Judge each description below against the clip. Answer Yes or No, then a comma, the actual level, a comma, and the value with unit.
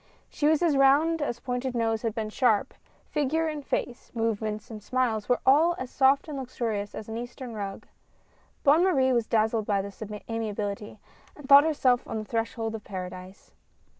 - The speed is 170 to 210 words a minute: Yes, average, 180 wpm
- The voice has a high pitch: Yes, high, 240 Hz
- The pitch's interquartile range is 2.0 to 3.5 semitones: No, average, 4.1 semitones